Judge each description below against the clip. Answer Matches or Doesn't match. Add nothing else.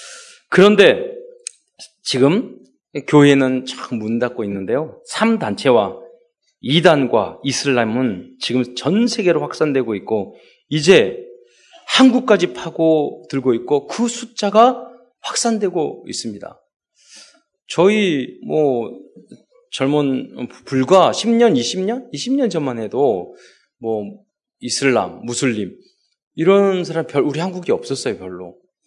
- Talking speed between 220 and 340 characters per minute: Doesn't match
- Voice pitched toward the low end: Doesn't match